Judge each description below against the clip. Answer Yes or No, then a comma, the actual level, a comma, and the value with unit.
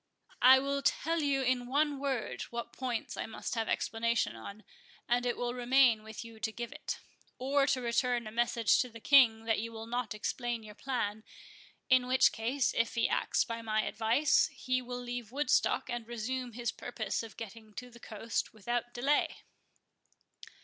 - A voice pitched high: Yes, high, 240 Hz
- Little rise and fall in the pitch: Yes, narrow, 2.3 semitones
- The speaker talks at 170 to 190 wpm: Yes, average, 180 wpm